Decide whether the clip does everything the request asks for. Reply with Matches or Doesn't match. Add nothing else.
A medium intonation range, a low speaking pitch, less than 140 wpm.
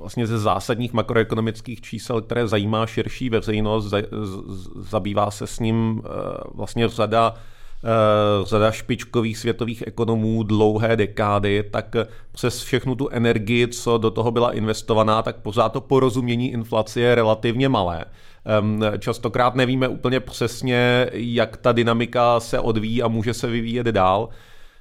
Doesn't match